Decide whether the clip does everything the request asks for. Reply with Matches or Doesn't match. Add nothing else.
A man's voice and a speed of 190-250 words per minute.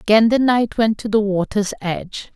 Doesn't match